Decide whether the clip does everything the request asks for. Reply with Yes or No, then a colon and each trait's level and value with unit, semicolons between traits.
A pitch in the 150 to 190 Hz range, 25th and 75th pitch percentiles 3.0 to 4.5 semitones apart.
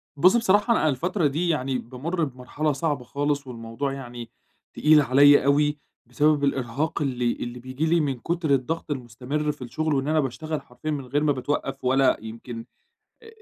No: medium, 140 Hz; average, 3.4 semitones